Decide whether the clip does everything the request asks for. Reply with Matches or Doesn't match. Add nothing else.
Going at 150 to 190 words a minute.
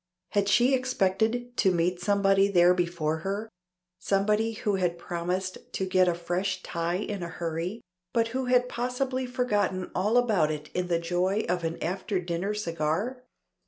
Matches